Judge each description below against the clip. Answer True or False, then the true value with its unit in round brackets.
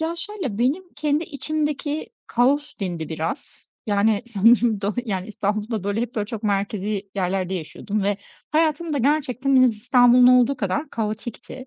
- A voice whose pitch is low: False (235 Hz)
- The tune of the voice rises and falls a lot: True (5.7 semitones)